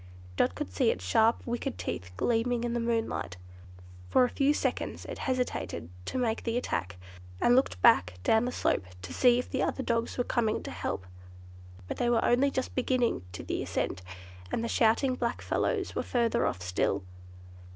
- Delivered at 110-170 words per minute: No, average, 185 wpm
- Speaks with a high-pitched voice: Yes, high, 235 Hz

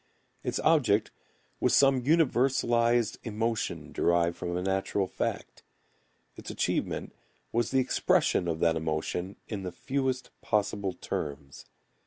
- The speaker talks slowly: Yes, slow, 120 wpm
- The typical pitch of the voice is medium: No, low, 105 Hz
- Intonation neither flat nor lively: No, wide, 6.2 semitones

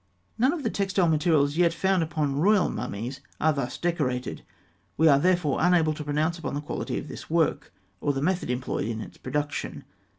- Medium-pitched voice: Yes, medium, 155 Hz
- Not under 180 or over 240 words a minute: Yes, average, 190 wpm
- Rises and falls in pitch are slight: No, average, 3.8 semitones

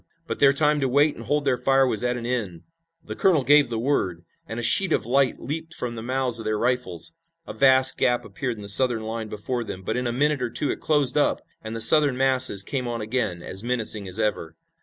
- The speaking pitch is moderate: No, low, 125 Hz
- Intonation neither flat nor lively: Yes, average, 3.6 semitones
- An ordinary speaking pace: No, fast, 245 wpm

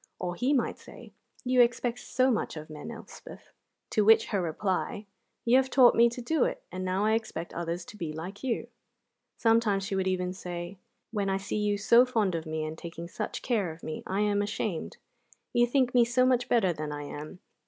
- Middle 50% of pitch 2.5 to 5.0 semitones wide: No, wide, 5.4 semitones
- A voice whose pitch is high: Yes, high, 205 Hz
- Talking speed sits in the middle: No, fast, 210 wpm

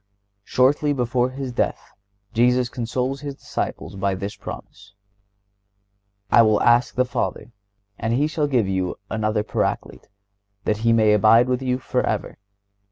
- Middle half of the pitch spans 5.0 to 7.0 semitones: No, average, 3.0 semitones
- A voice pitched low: Yes, low, 120 Hz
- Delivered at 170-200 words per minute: No, average, 140 wpm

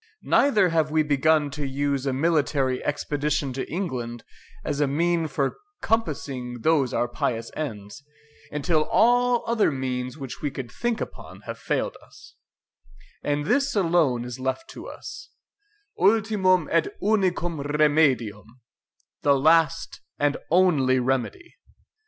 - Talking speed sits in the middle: No, slow, 130 wpm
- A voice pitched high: No, medium, 150 Hz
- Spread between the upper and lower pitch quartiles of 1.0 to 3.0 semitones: No, average, 4.8 semitones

